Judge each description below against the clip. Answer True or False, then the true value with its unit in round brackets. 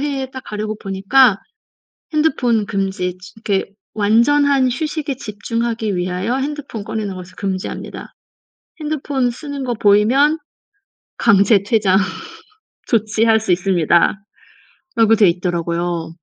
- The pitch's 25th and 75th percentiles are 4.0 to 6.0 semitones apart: True (5.3 semitones)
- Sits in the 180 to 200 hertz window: False (215 Hz)